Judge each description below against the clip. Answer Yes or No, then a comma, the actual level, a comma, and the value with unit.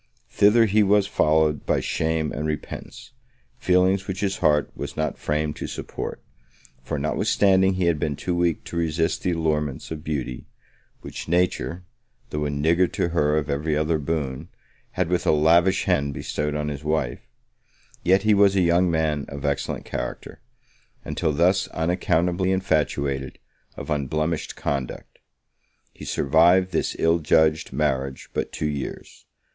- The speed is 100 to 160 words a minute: Yes, average, 155 wpm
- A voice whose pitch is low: Yes, very low, 80 Hz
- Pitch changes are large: No, average, 3.2 semitones